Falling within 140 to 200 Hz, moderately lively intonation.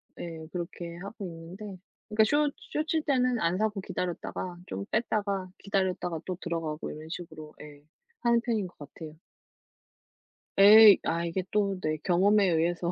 Yes: medium, 185 Hz; average, 4.1 semitones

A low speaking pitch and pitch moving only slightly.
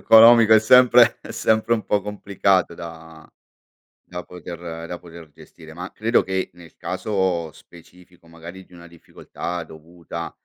No: very low, 90 Hz; average, 3.8 semitones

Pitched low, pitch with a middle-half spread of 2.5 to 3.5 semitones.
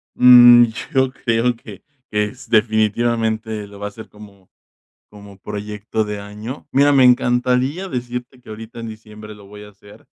Yes: low, 110 Hz; average, 2.9 semitones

